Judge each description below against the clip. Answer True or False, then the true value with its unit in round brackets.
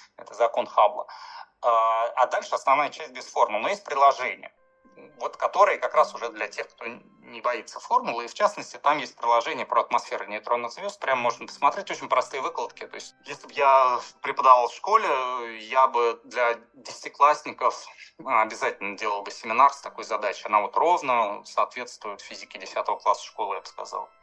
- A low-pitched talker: True (130 Hz)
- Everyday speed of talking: False (170 wpm)